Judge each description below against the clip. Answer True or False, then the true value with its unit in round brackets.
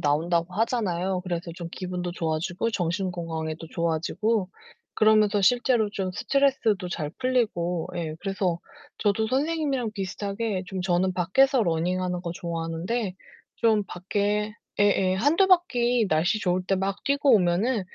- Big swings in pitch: False (4.5 semitones)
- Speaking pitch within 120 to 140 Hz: False (190 Hz)